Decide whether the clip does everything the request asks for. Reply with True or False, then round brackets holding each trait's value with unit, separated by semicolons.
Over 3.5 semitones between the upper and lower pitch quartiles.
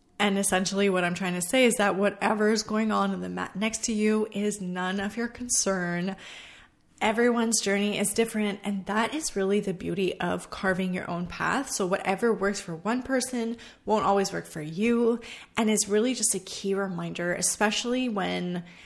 False (3.1 semitones)